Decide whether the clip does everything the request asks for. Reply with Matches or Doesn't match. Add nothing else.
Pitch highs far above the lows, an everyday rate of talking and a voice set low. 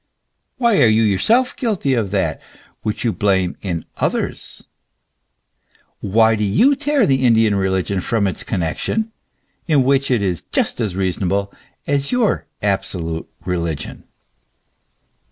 Doesn't match